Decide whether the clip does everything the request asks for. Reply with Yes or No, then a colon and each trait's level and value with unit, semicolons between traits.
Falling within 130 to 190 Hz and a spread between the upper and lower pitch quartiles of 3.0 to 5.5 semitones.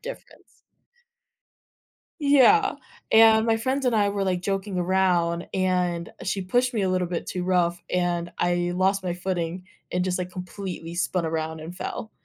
No: medium, 185 Hz; narrow, 2.4 semitones